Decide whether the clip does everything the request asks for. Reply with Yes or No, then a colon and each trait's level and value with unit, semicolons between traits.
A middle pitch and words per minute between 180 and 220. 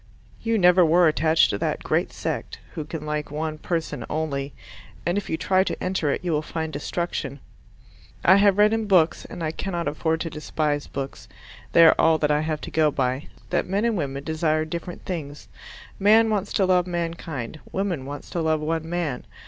Yes: medium, 160 Hz; average, 195 wpm